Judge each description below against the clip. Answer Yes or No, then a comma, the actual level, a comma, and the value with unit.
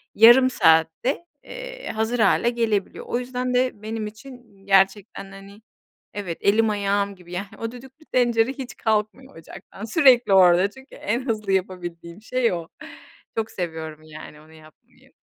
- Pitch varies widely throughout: No, average, 4.6 semitones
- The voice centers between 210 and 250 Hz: Yes, high, 215 Hz